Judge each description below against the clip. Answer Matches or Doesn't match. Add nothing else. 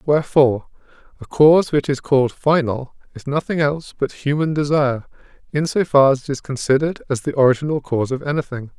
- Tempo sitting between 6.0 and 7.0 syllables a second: Matches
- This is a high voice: Doesn't match